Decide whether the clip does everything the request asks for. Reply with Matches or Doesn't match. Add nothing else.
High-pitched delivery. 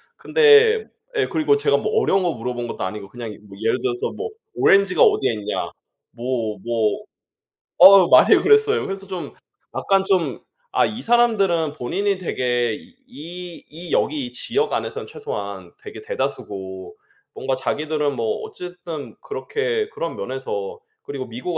Doesn't match